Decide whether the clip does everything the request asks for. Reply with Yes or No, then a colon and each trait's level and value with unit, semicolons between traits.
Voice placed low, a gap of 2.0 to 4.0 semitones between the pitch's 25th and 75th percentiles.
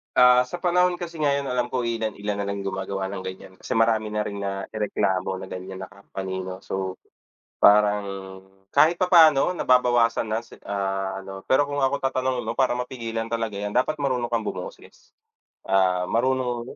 No: low, 115 Hz; average, 4.9 semitones